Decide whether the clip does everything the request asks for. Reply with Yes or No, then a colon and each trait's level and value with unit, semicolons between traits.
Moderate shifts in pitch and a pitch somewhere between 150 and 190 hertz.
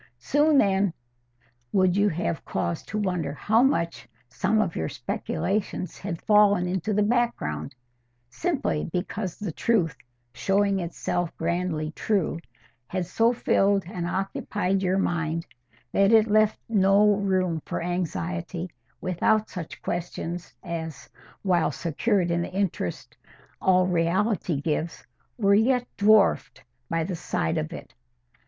Yes: average, 3.5 semitones; medium, 185 Hz